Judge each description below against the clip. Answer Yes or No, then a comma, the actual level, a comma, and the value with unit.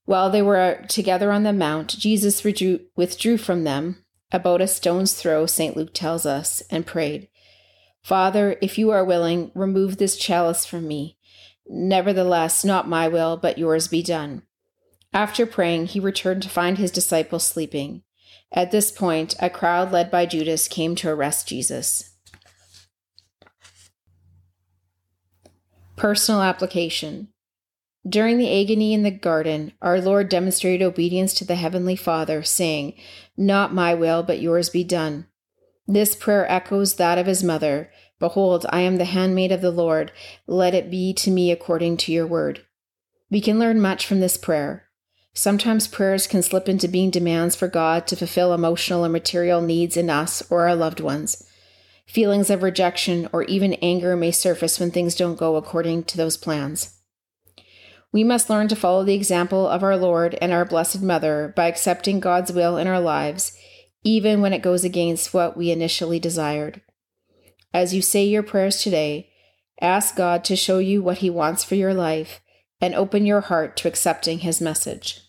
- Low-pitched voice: No, medium, 175 Hz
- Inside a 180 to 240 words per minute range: No, average, 165 wpm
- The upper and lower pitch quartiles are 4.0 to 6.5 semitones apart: No, average, 3.0 semitones